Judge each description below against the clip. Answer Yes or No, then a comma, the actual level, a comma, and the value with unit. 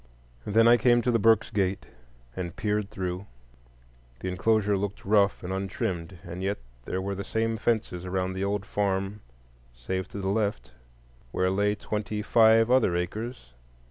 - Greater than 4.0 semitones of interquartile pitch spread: No, average, 2.8 semitones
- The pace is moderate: Yes, average, 160 wpm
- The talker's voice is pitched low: Yes, low, 100 Hz